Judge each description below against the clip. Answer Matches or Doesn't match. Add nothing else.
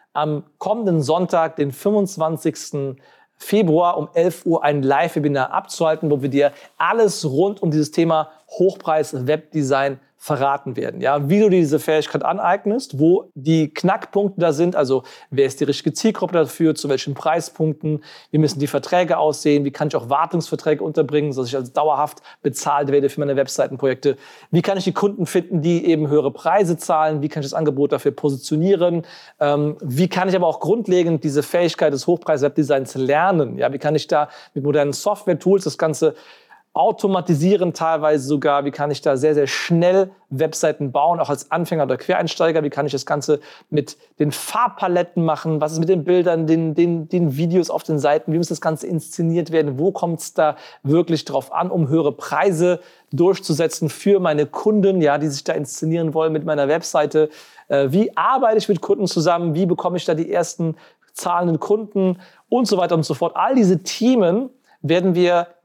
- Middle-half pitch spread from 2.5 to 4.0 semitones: Matches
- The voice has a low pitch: Doesn't match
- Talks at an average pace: Matches